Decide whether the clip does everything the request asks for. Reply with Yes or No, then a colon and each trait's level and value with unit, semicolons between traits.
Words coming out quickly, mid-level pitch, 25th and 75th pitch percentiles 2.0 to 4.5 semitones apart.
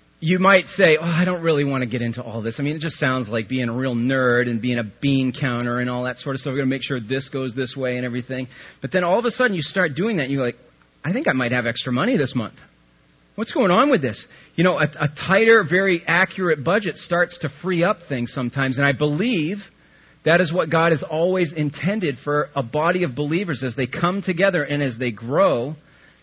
No: fast, 250 wpm; medium, 145 Hz; wide, 5.4 semitones